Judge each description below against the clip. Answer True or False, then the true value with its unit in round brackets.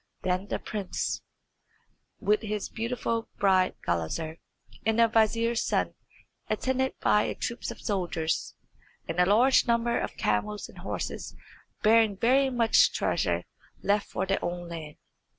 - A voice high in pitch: True (210 Hz)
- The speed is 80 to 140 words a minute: True (135 wpm)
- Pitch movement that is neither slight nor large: True (4.2 semitones)